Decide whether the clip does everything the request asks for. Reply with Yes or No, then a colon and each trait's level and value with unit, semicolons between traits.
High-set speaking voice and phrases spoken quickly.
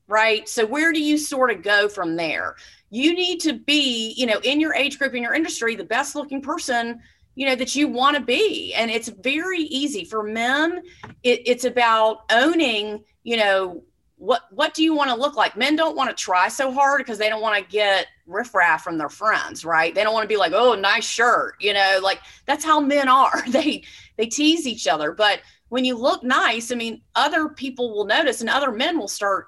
Yes: very high, 250 Hz; fast, 220 wpm